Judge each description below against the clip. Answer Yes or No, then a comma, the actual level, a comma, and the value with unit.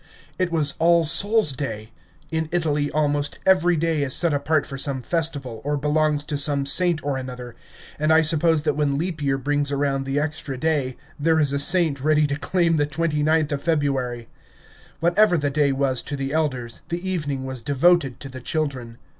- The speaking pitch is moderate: Yes, medium, 145 Hz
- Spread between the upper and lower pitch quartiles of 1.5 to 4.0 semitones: Yes, average, 2.8 semitones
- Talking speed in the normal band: Yes, average, 190 wpm